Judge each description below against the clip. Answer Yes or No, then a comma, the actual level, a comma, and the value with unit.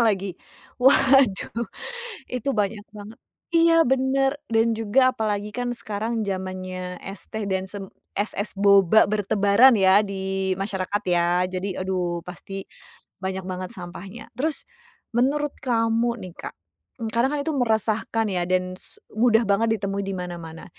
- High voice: Yes, high, 205 Hz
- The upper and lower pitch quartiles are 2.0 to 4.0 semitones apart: Yes, average, 3.7 semitones